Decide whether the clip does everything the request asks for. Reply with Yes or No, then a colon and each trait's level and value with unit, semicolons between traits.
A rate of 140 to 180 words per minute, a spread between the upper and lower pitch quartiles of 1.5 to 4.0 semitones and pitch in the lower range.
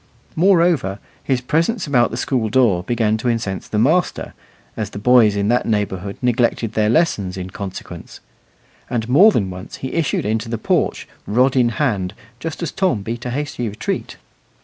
No: average, 170 wpm; average, 4.4 semitones; low, 115 Hz